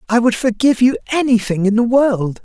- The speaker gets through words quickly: No, average, 195 wpm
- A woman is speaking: No, male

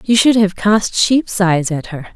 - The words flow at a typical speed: No, fast, 225 wpm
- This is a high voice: Yes, high, 200 Hz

